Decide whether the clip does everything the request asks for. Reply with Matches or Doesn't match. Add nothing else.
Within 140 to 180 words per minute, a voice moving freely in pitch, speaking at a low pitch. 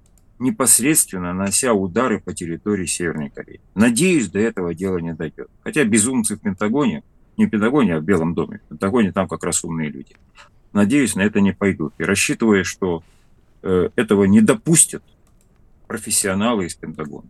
Matches